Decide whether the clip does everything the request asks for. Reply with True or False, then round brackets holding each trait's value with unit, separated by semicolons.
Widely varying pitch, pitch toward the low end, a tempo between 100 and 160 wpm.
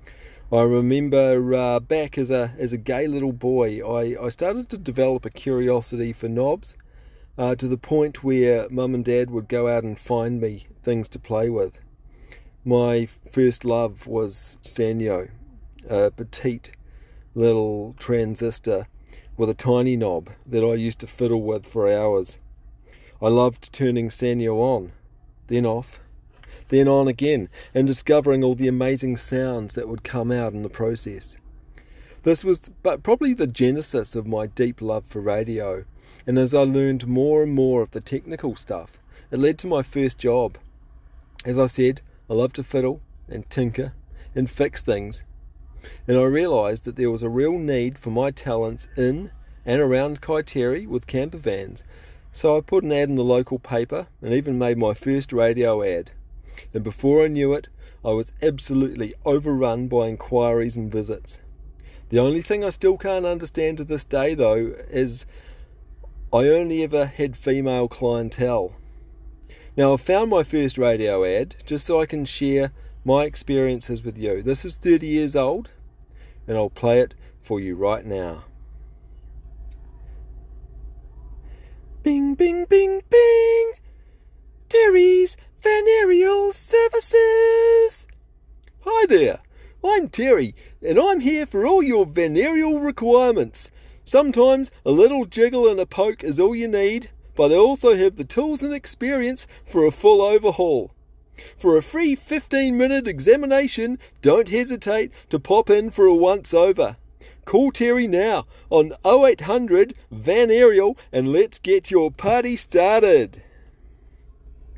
True (7.8 semitones; 130 Hz; 150 wpm)